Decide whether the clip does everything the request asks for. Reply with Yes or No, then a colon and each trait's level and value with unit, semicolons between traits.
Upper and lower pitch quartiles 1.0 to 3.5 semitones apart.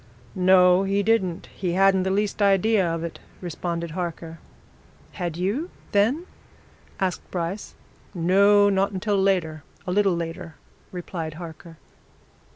Yes: average, 2.7 semitones